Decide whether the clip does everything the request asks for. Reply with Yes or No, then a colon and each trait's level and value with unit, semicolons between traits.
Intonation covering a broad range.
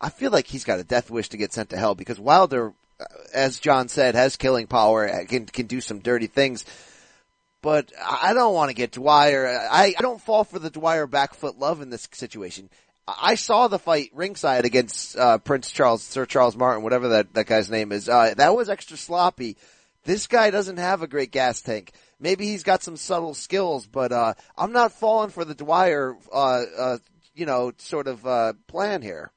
Yes: wide, 6.3 semitones